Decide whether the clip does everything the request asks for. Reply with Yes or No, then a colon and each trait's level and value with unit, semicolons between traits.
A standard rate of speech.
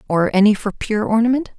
Yes: average, 190 wpm